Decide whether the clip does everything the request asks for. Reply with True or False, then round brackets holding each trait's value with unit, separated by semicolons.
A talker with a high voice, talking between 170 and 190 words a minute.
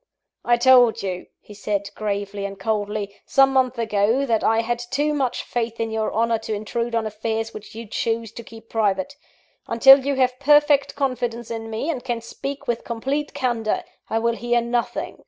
True (230 Hz; 185 wpm)